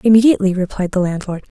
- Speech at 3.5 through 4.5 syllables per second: No, 7.3 syllables/s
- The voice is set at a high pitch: Yes, high, 195 Hz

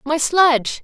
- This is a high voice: Yes, very high, 295 Hz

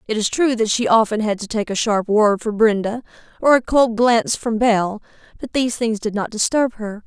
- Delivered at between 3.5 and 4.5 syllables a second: No, 5.4 syllables/s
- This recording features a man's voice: No, female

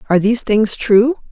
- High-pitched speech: Yes, high, 225 Hz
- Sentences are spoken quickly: No, average, 185 wpm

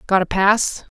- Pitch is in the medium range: No, high, 195 Hz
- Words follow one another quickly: No, average, 190 wpm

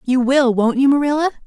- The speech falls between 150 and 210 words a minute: Yes, fast, 205 wpm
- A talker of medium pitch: No, very high, 265 Hz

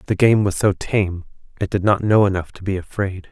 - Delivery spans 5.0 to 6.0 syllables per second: Yes, 5.4 syllables/s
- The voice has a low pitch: Yes, low, 100 Hz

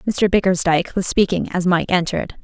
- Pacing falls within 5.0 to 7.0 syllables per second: Yes, 5.9 syllables/s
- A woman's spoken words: Yes, female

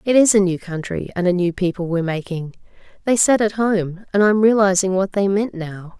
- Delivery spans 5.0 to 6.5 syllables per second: Yes, 5.3 syllables/s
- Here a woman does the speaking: Yes, female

